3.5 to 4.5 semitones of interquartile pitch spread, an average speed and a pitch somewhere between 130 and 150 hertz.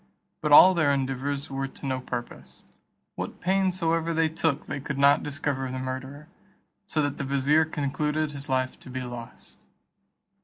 No: average, 2.8 semitones; average, 165 wpm; medium, 140 Hz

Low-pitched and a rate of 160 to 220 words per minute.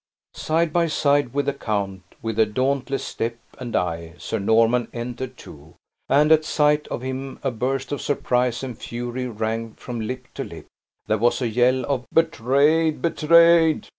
Yes: low, 125 Hz; average, 165 wpm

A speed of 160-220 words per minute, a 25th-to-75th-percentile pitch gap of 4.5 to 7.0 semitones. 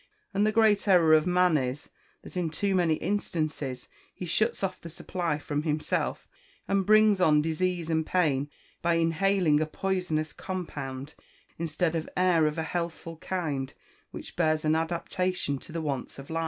No: average, 165 wpm; average, 3.0 semitones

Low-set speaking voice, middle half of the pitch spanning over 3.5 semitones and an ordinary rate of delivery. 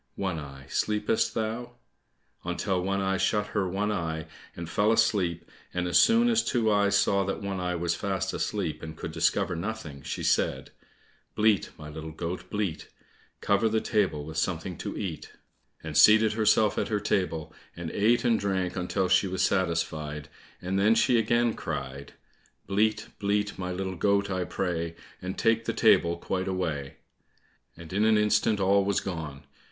Yes: very low, 95 Hz; average, 3.9 semitones; average, 170 wpm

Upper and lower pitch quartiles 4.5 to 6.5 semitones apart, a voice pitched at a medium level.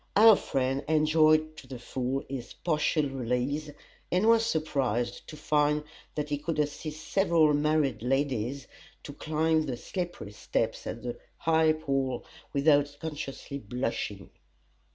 No: average, 3.0 semitones; medium, 145 Hz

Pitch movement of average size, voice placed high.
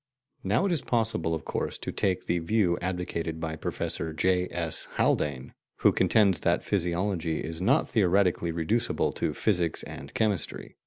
No: average, 3.9 semitones; very low, 90 Hz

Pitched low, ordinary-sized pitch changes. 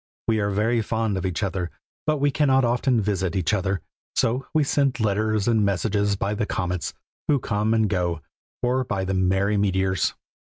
Yes: low, 105 Hz; average, 3.5 semitones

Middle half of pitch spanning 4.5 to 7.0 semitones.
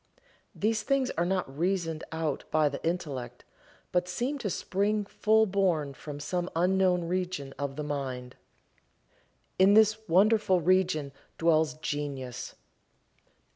Yes: average, 4.8 semitones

